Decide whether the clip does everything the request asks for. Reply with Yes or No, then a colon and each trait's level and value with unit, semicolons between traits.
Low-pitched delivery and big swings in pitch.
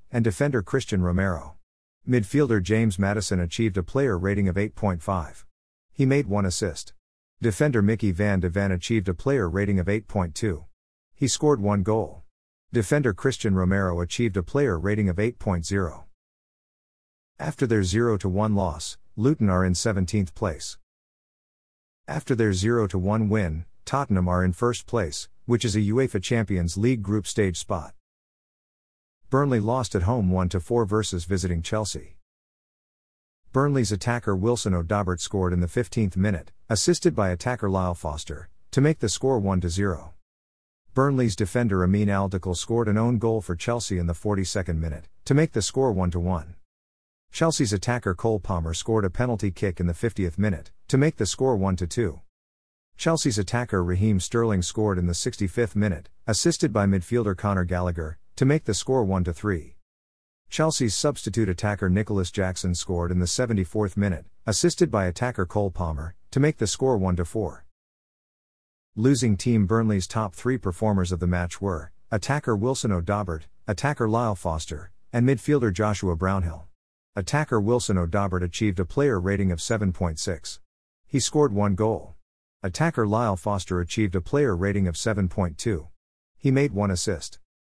No: low, 100 Hz; average, 4.4 semitones